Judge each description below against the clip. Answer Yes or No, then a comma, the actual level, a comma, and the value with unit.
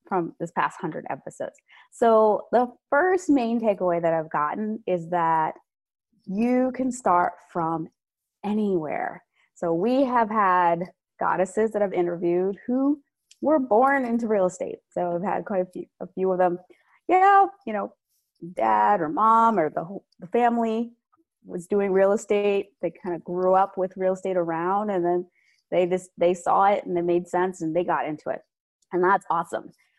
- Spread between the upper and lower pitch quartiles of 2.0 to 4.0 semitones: No, average, 4.7 semitones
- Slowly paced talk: No, average, 175 wpm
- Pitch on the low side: No, high, 190 Hz